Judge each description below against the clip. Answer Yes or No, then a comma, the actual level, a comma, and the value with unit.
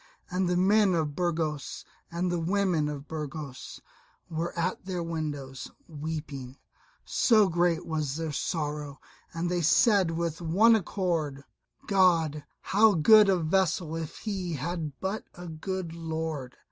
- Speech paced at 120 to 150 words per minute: Yes, slow, 135 wpm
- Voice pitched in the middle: Yes, medium, 165 Hz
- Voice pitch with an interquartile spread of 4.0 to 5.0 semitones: No, average, 3.1 semitones